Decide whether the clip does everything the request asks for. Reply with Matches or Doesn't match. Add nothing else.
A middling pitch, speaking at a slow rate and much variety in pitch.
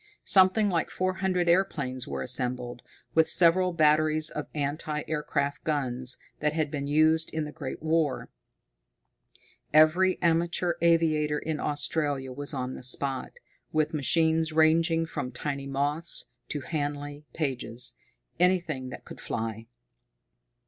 Doesn't match